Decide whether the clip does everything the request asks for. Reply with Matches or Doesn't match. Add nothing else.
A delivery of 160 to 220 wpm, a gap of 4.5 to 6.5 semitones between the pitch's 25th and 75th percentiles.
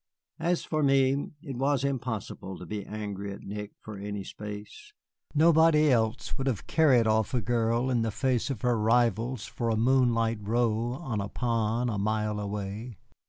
Doesn't match